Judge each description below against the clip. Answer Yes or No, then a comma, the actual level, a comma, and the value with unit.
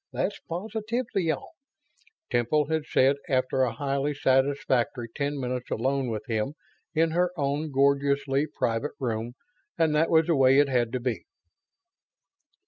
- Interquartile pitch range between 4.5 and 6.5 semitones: No, average, 3.3 semitones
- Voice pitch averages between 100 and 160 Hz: Yes, medium, 140 Hz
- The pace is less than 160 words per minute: Yes, average, 140 wpm